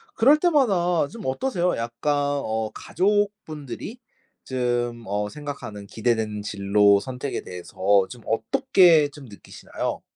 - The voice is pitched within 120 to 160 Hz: Yes, low, 135 Hz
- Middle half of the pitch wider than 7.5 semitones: Yes, wide, 8.2 semitones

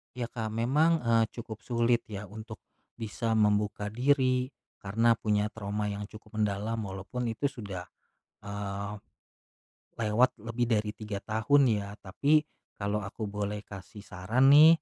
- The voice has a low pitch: Yes, low, 110 Hz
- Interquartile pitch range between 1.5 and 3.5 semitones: Yes, narrow, 2.5 semitones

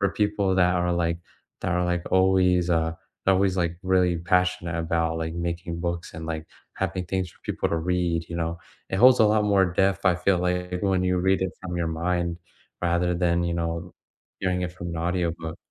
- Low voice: Yes, very low, 90 Hz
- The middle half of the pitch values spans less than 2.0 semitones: Yes, narrow, 1.6 semitones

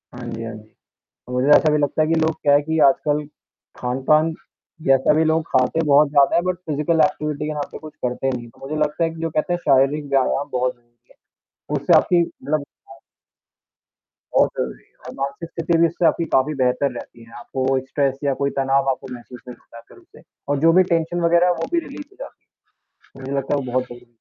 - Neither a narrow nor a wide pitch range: Yes, average, 3.6 semitones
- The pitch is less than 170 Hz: Yes, medium, 140 Hz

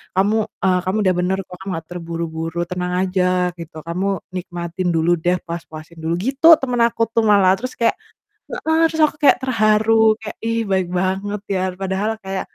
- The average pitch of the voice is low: No, high, 190 Hz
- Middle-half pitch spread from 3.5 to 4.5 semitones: Yes, average, 3.8 semitones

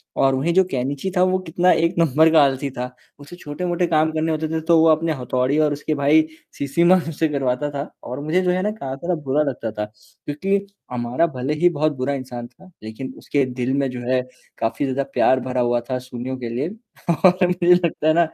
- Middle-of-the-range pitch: Yes, medium, 145 Hz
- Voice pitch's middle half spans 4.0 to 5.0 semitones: Yes, average, 4.5 semitones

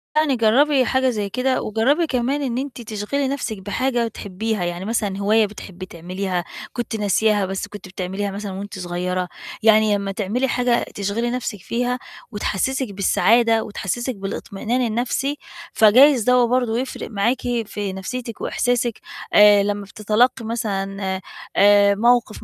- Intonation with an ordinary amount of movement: Yes, average, 3.7 semitones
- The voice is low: No, high, 220 Hz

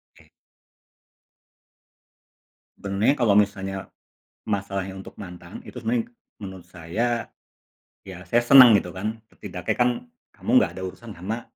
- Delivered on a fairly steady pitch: No, average, 3.8 semitones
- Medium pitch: No, low, 100 Hz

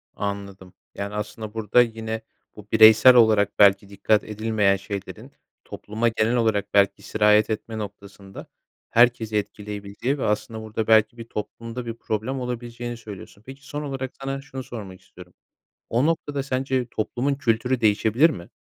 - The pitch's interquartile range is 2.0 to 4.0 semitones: Yes, average, 3.0 semitones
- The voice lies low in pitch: Yes, low, 110 Hz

